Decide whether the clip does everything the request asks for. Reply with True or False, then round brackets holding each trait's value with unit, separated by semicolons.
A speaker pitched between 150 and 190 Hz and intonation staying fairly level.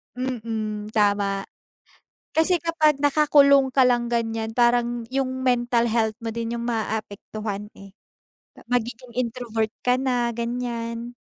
False (235 Hz; 2.3 semitones)